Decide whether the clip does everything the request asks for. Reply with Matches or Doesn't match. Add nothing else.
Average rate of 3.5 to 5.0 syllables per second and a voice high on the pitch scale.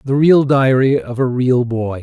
Doesn't match